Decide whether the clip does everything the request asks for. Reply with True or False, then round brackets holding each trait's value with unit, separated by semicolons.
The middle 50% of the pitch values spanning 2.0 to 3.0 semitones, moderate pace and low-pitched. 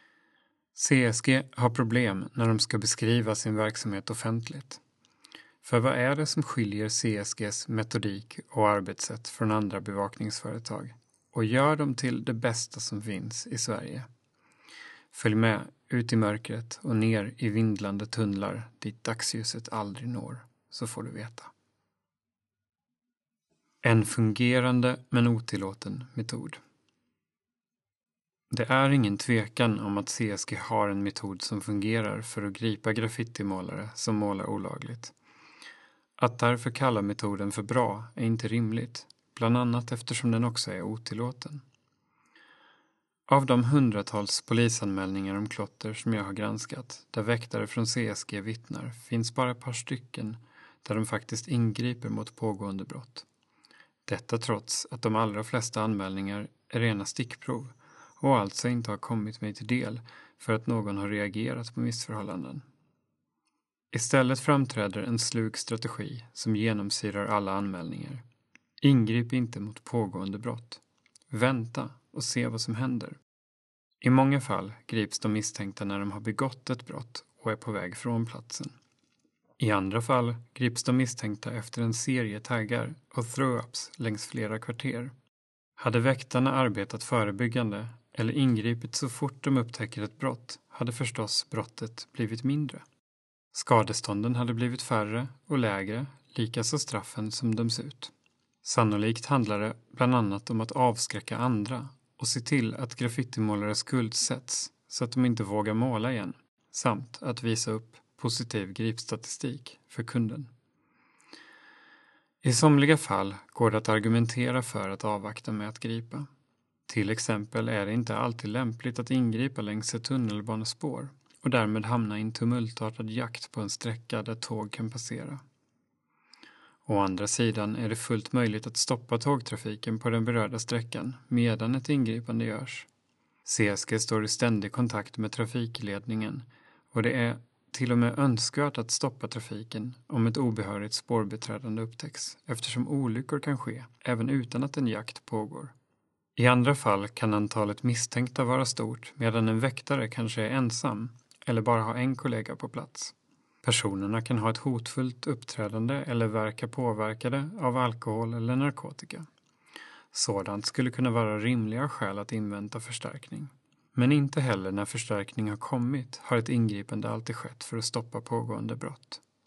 True (2.6 semitones; 145 wpm; 115 Hz)